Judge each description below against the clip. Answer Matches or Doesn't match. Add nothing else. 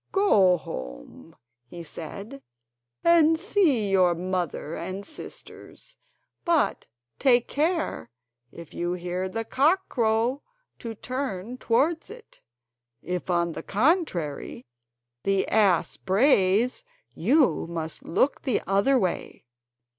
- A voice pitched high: Matches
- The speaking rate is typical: Doesn't match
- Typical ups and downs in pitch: Doesn't match